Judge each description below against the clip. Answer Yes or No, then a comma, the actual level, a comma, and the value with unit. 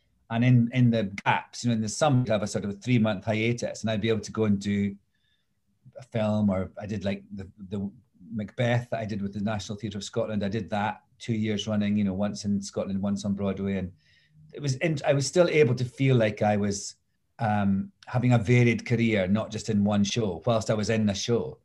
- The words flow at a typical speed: No, fast, 245 wpm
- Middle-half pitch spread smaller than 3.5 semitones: Yes, narrow, 2.6 semitones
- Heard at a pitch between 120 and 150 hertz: No, low, 110 Hz